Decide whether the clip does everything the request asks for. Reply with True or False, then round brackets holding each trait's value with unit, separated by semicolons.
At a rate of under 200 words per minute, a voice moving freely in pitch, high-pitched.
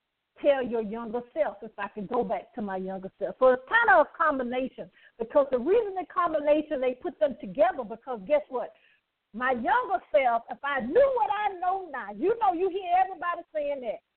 False (205 wpm; 7.0 semitones; 295 Hz)